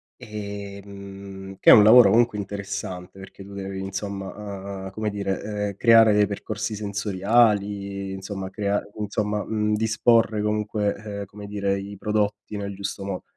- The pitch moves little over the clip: Yes, narrow, 1.4 semitones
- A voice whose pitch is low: Yes, low, 100 Hz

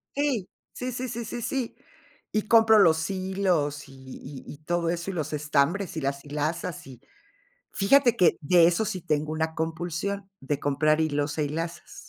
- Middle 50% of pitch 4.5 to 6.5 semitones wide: Yes, average, 4.8 semitones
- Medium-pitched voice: Yes, medium, 165 Hz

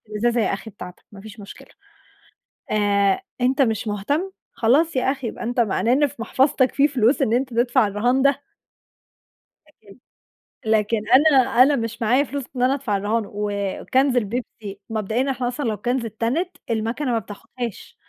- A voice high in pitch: Yes, high, 235 Hz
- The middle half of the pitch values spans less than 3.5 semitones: No, average, 3.8 semitones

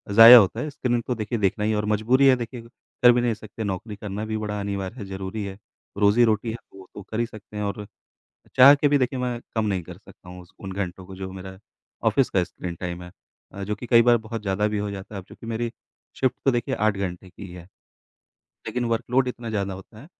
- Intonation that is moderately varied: Yes, average, 3.5 semitones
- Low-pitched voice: Yes, low, 105 Hz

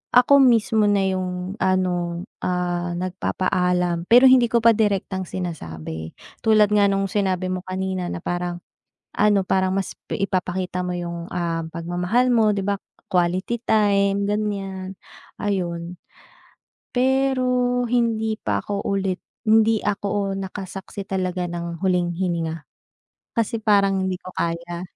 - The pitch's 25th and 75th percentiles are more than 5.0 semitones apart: No, average, 2.8 semitones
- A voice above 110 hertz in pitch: Yes, high, 190 Hz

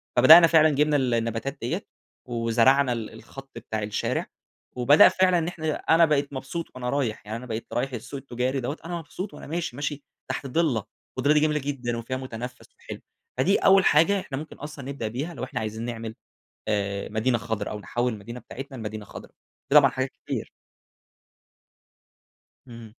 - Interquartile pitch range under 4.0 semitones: No, average, 4.3 semitones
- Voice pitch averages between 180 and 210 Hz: No, low, 130 Hz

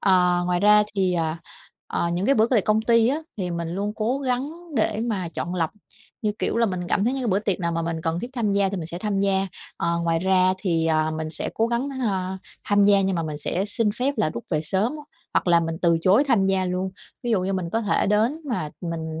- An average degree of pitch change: Yes, average, 4.1 semitones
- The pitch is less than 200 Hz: Yes, high, 190 Hz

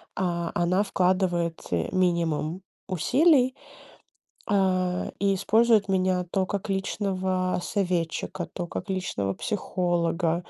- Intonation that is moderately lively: No, narrow, 2.1 semitones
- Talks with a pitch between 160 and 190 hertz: Yes, medium, 185 Hz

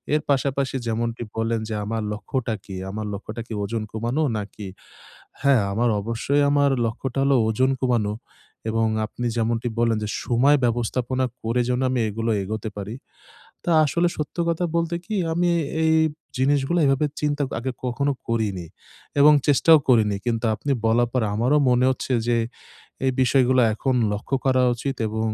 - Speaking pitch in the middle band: No, low, 120 Hz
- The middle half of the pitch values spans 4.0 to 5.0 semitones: No, average, 3.5 semitones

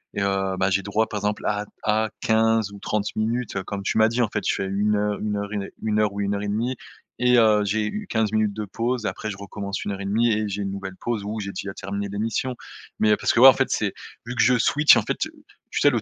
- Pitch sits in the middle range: No, low, 105 Hz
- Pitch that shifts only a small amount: Yes, narrow, 1.8 semitones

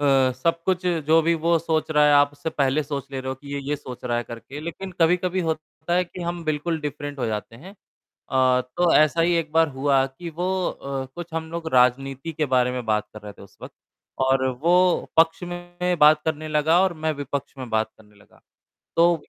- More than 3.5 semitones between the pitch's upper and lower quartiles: Yes, average, 4.0 semitones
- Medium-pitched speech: Yes, medium, 150 Hz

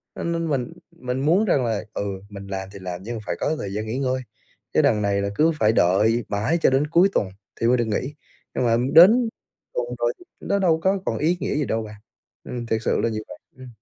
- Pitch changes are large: Yes, wide, 7.2 semitones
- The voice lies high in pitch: No, low, 125 Hz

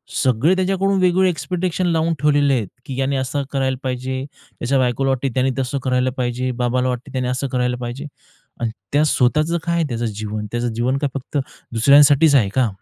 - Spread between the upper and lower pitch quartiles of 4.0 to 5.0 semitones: No, average, 3.1 semitones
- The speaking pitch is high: No, low, 130 Hz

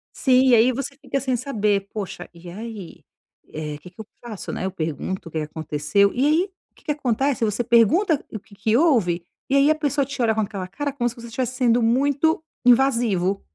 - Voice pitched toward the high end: Yes, high, 230 Hz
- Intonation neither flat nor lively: No, wide, 5.7 semitones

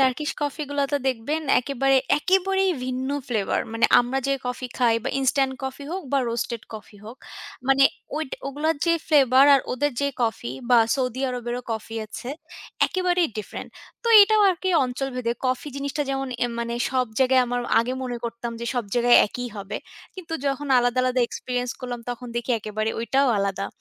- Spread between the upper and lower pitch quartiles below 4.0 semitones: Yes, average, 2.8 semitones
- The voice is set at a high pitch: Yes, very high, 255 Hz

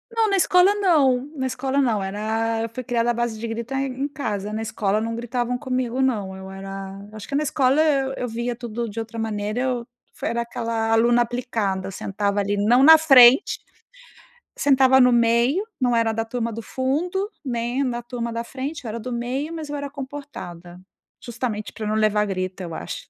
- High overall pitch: Yes, high, 240 Hz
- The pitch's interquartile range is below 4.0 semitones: Yes, average, 3.4 semitones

